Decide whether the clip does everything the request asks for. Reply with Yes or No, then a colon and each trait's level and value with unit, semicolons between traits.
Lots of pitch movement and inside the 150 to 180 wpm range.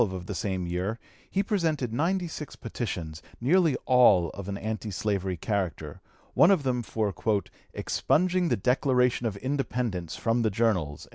Yes: wide, 6.1 semitones; average, 165 wpm